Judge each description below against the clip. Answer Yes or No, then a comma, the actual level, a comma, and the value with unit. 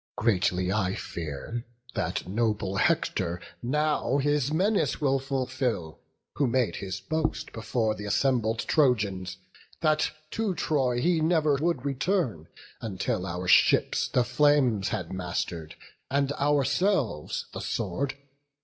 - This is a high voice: No, low, 125 Hz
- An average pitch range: No, wide, 7.1 semitones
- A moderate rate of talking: No, slow, 120 wpm